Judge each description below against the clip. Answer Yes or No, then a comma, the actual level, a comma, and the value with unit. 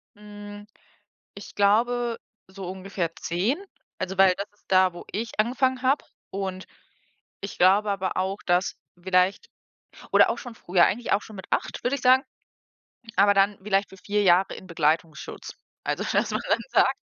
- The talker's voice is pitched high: Yes, high, 195 Hz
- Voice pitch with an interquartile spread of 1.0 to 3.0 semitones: Yes, narrow, 2.4 semitones